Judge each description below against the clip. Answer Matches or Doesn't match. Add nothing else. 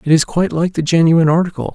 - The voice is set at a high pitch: Doesn't match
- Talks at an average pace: Doesn't match